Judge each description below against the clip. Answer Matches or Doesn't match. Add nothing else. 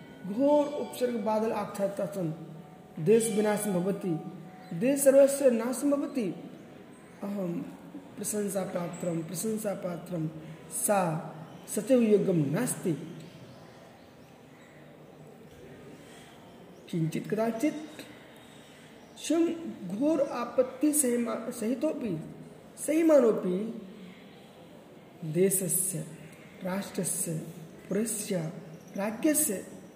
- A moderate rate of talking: Doesn't match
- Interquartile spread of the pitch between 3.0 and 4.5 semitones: Doesn't match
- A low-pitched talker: Doesn't match